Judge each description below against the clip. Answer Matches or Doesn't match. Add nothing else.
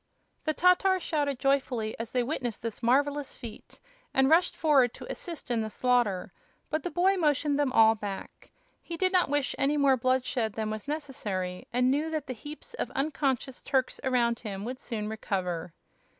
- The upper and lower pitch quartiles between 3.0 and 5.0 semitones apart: Matches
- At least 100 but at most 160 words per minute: Doesn't match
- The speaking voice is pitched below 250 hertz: Doesn't match